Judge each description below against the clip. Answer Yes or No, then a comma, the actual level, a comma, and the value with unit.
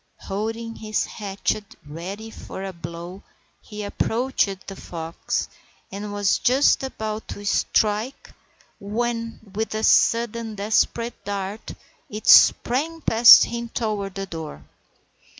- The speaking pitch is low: No, high, 215 Hz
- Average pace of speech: No, slow, 115 wpm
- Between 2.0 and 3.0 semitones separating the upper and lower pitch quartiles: Yes, average, 2.7 semitones